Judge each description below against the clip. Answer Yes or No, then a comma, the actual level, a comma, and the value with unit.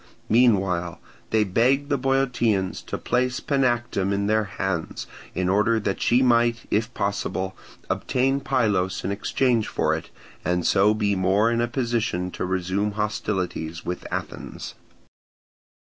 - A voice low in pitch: Yes, low, 105 Hz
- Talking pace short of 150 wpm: Yes, slow, 135 wpm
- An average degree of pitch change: Yes, average, 4.1 semitones